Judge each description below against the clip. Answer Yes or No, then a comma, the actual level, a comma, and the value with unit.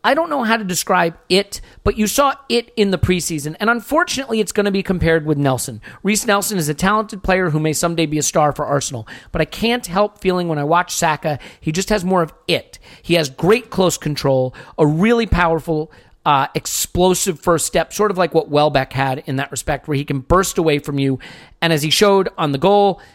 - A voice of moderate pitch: Yes, medium, 170 Hz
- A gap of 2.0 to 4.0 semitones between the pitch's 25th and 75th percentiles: No, average, 5.0 semitones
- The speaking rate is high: Yes, fast, 225 wpm